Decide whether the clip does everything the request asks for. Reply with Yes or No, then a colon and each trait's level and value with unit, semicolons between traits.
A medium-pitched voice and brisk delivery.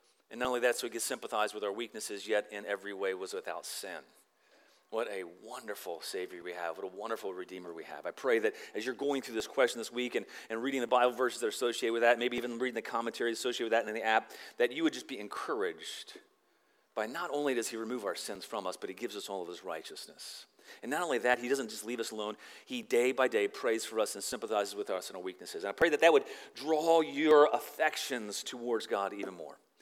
Yes: medium, 145 Hz; fast, 250 wpm